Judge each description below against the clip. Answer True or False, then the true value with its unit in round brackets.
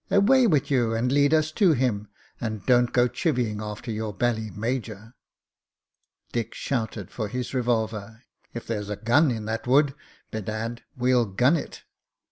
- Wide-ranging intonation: False (3.0 semitones)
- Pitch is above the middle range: False (120 Hz)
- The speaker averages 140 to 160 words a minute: True (155 wpm)